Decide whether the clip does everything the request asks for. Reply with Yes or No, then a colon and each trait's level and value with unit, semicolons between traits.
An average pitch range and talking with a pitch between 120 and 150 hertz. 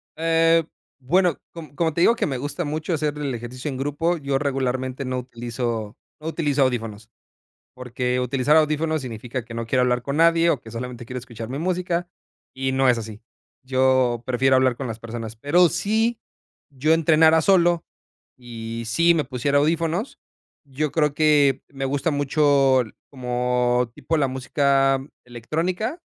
Yes: average, 4.2 semitones; low, 135 Hz